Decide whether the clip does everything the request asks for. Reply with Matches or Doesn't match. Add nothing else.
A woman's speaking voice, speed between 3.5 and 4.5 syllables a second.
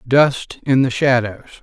Doesn't match